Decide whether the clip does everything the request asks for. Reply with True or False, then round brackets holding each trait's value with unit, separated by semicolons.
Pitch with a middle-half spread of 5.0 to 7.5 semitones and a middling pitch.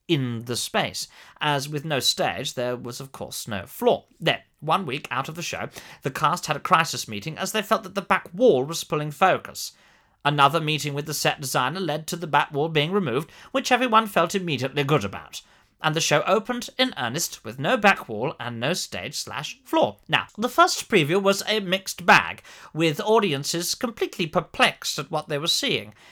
True (5.5 semitones; 165 Hz)